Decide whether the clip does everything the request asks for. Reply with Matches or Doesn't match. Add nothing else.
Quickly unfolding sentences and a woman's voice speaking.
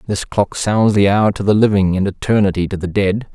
Doesn't match